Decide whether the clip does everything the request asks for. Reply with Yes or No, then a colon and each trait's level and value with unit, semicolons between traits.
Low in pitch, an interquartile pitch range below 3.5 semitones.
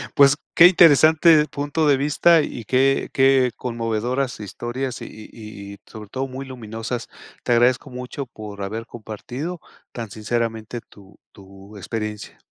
No: low, 120 Hz; average, 4.0 semitones